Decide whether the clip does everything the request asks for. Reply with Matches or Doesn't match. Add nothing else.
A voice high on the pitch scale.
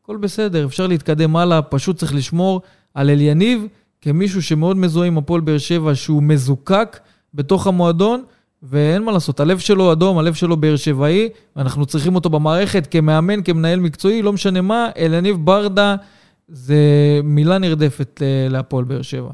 Doesn't match